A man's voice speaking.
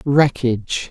Yes: male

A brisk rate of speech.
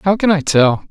Yes: fast, 265 wpm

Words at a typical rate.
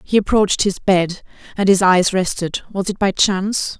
Yes: average, 190 wpm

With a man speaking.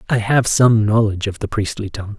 Yes: male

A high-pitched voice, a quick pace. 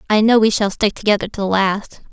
Yes: high, 205 Hz; fast, 255 wpm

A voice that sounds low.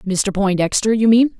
No: high, 210 Hz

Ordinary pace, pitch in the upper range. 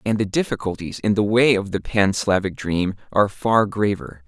No: average, 195 wpm; low, 100 Hz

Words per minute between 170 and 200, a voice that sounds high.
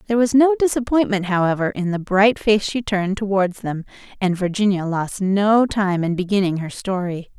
Yes: average, 180 wpm; high, 200 Hz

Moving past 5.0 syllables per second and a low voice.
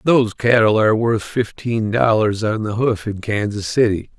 No: 4.7 syllables/s; low, 110 Hz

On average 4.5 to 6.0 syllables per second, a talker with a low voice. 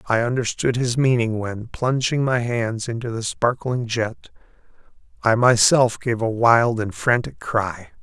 No: 4.1 syllables/s; low, 115 Hz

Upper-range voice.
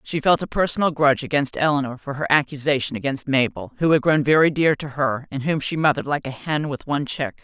No: medium, 140 Hz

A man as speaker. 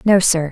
No: female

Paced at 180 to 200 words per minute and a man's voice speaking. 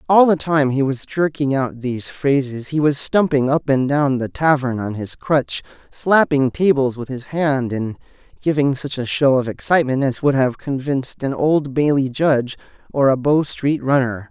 Yes: average, 190 wpm; male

